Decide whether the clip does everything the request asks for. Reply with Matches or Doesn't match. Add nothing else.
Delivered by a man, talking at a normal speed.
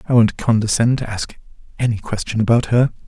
Matches